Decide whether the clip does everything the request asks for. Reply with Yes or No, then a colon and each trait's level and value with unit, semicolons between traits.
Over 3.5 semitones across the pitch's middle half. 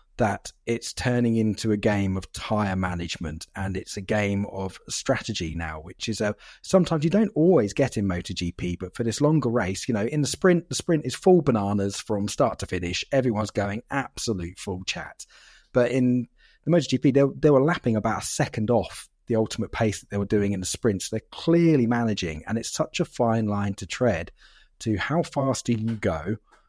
Yes: average, 5.1 semitones